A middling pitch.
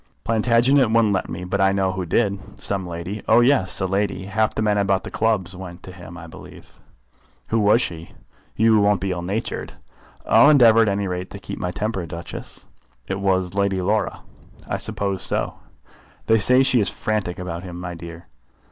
No: low, 100 Hz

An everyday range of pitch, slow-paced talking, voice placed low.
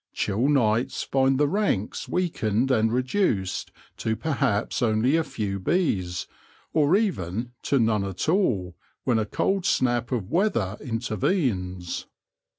No: wide, 6.4 semitones; slow, 130 wpm; low, 120 Hz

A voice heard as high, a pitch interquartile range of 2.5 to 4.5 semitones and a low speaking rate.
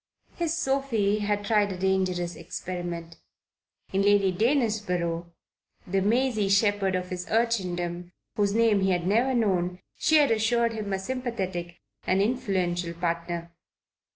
Yes: high, 195 Hz; average, 4.1 semitones; slow, 130 wpm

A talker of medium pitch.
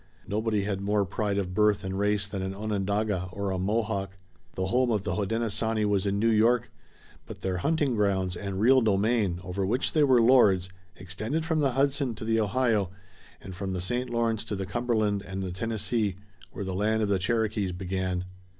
No: low, 105 Hz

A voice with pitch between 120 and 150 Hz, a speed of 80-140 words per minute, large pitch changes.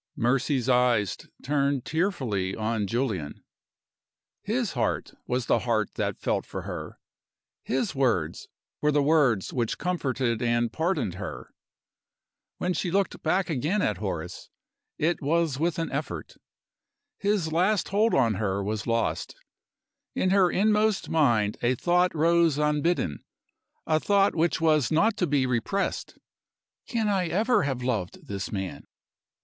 Yes: medium, 140 Hz; slow, 135 wpm; wide, 7.1 semitones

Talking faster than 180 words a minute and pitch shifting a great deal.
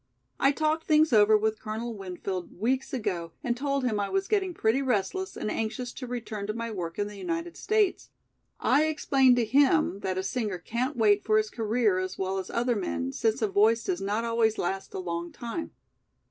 No: average, 200 wpm; average, 4.8 semitones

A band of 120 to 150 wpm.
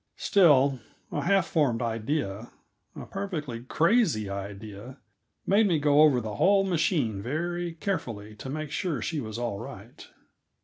Yes: average, 140 wpm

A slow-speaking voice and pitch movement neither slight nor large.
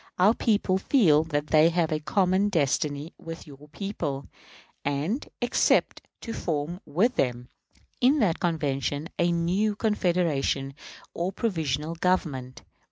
Yes: slow, 125 wpm; average, 4.7 semitones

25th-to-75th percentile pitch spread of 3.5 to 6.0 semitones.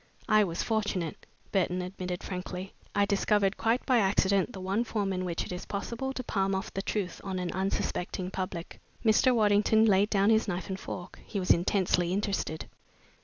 No: narrow, 2.4 semitones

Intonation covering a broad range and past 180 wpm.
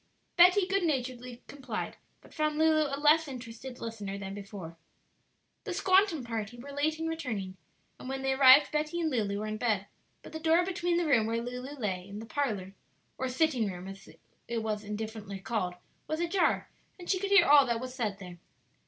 Yes: wide, 6.6 semitones; average, 195 wpm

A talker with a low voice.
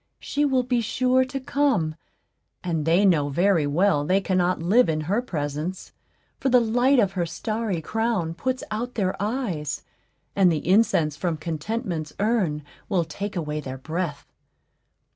No: medium, 185 Hz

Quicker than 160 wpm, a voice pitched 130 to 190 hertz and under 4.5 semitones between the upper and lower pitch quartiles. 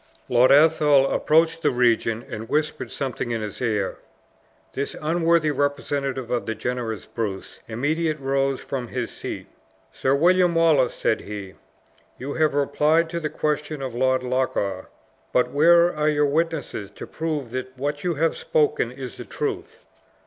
No: average, 155 wpm; medium, 140 Hz; average, 4.1 semitones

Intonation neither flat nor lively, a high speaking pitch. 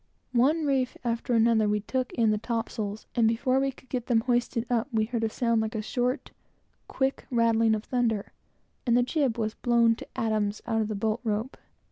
No: narrow, 2.0 semitones; high, 230 Hz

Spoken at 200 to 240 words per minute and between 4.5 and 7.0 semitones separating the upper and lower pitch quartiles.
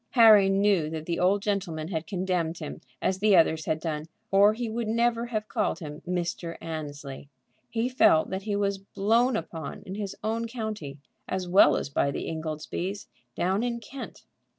No: average, 175 wpm; average, 5.1 semitones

